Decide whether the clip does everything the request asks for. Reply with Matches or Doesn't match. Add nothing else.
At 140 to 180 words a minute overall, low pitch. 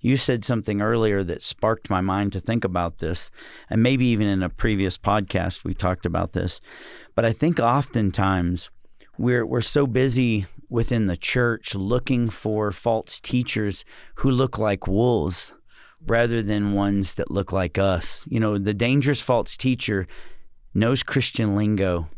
Matches